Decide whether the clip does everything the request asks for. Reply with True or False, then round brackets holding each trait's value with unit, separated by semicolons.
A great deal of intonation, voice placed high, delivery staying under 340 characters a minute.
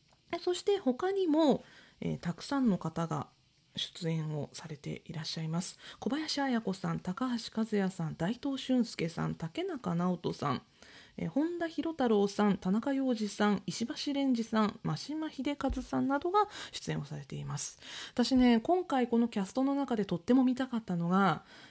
True (8.0 semitones; 225 Hz; 320 characters per minute)